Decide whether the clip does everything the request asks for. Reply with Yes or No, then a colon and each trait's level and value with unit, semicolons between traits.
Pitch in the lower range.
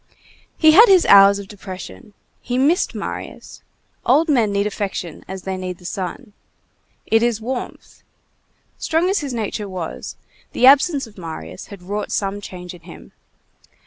No: high, 205 Hz